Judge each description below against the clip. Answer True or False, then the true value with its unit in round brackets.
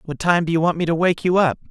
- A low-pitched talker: False (170 Hz)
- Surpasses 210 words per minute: True (315 wpm)